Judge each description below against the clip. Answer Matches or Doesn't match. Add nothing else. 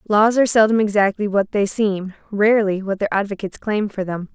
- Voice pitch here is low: Doesn't match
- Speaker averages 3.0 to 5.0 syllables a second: Doesn't match